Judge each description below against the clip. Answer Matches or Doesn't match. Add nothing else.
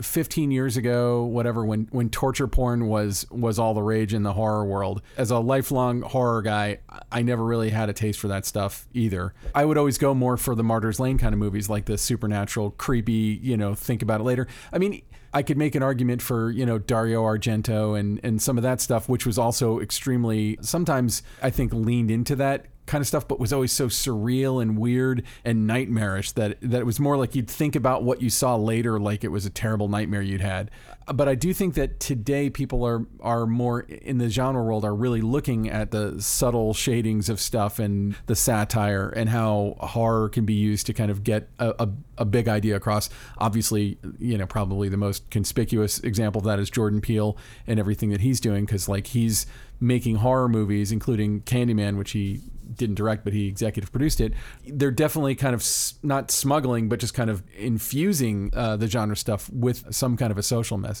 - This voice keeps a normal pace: Doesn't match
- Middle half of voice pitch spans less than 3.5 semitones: Matches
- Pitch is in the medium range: Doesn't match